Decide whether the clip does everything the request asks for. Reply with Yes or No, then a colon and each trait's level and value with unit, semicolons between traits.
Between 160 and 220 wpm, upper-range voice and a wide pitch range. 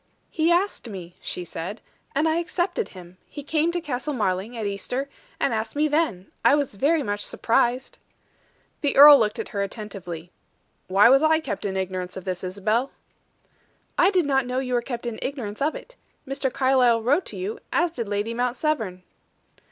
Yes: average, 185 wpm; high, 245 Hz; wide, 6.8 semitones